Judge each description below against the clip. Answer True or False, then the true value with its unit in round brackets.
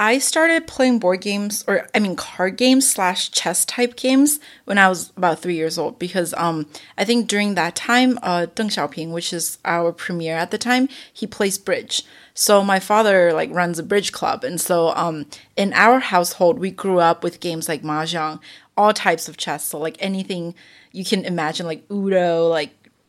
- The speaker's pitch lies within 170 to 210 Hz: True (185 Hz)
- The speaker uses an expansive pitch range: False (4.2 semitones)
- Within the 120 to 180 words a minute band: False (195 wpm)